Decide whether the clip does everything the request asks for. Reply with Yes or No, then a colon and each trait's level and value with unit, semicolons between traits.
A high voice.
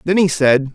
No: medium, 155 Hz